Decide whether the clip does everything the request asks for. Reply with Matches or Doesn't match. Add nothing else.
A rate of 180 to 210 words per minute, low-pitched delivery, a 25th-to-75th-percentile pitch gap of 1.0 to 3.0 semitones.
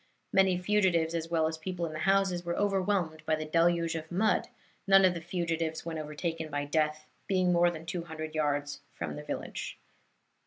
Doesn't match